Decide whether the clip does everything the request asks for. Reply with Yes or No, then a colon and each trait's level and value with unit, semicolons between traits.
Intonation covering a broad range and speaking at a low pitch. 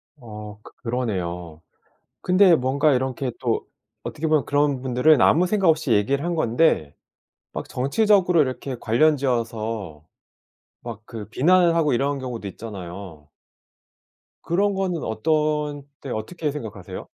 Yes: wide, 6.1 semitones; low, 130 Hz